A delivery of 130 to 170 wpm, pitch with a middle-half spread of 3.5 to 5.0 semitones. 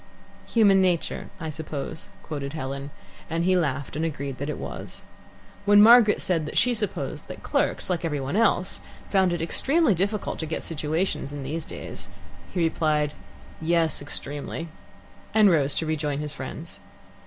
Yes: average, 160 wpm; average, 4.2 semitones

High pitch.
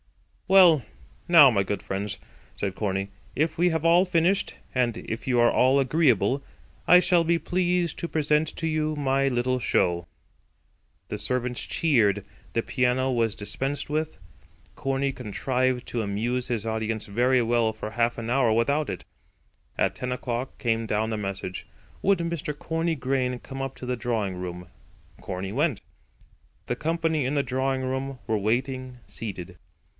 No: low, 125 Hz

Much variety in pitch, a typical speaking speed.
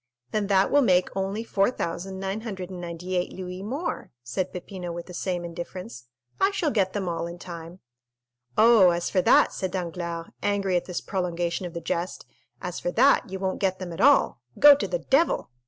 No: narrow, 2.4 semitones; average, 175 wpm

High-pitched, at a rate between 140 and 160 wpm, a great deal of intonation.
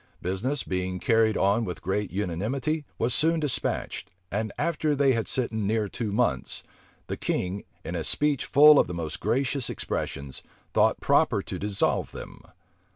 No: low, 110 Hz; average, 155 wpm; wide, 6.3 semitones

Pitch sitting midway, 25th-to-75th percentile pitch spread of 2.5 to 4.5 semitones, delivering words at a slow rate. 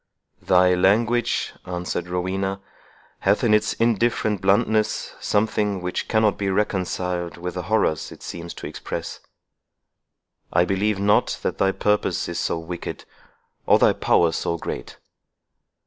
No: very low, 95 Hz; average, 2.9 semitones; slow, 130 wpm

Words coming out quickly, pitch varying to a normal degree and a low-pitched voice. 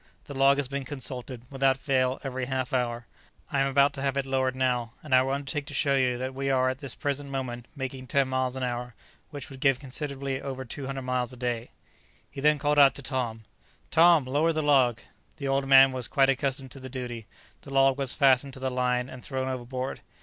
No: fast, 225 wpm; narrow, 1.4 semitones; low, 130 Hz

